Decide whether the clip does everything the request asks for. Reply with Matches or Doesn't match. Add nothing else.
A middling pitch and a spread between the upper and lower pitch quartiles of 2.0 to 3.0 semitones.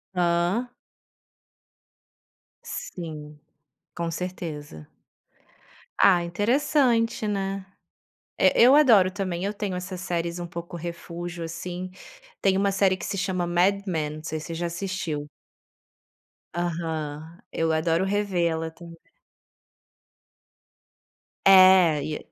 Matches